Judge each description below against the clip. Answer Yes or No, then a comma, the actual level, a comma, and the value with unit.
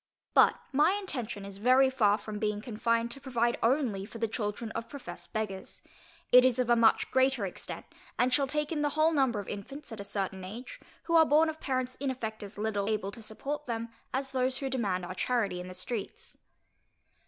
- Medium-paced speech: No, fast, 210 wpm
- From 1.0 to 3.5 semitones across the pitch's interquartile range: No, average, 4.3 semitones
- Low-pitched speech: No, high, 235 Hz